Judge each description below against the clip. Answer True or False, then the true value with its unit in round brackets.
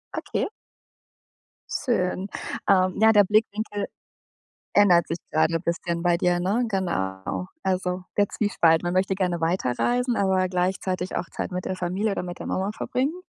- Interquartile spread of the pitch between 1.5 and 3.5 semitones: True (2.6 semitones)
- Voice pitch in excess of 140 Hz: True (185 Hz)